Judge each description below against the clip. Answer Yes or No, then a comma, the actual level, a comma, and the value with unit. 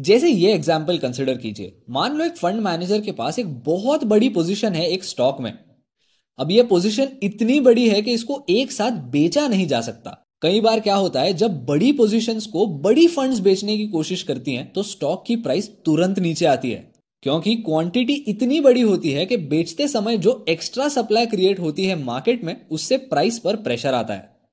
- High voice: Yes, high, 205 Hz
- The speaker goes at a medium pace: No, fast, 200 wpm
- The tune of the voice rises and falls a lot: Yes, wide, 6.4 semitones